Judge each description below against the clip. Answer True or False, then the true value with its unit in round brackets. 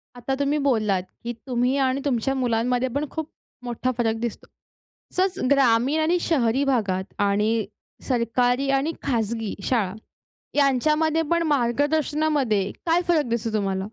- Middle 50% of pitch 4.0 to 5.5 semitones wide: True (4.4 semitones)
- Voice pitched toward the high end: True (250 Hz)